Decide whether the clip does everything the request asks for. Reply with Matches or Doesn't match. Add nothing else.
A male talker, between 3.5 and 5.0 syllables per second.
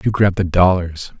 Matches